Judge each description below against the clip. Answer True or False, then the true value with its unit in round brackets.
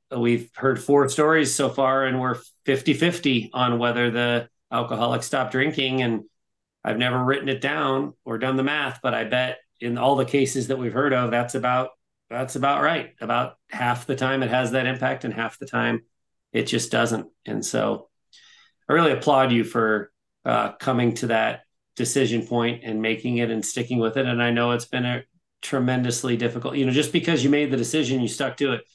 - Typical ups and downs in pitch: False (2.1 semitones)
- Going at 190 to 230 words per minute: True (200 wpm)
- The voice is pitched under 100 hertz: False (125 Hz)